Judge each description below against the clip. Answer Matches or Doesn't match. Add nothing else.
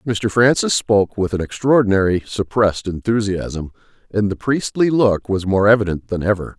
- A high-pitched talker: Doesn't match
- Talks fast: Doesn't match